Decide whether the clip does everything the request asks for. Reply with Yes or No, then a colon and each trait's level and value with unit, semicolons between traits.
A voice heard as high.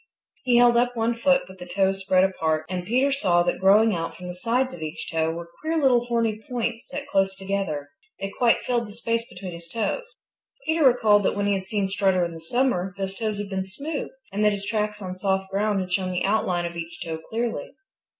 Yes: high, 200 Hz